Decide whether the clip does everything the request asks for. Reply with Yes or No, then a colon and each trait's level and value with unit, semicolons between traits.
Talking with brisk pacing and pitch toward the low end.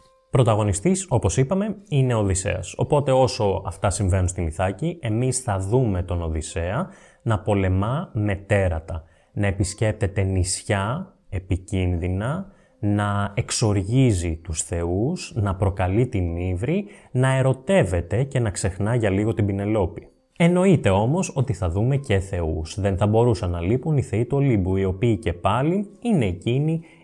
No: average, 140 wpm; low, 105 Hz